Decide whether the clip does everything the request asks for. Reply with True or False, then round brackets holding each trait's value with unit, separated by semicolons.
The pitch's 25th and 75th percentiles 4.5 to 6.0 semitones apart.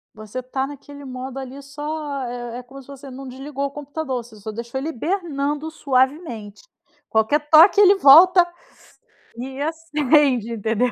False (3.2 semitones)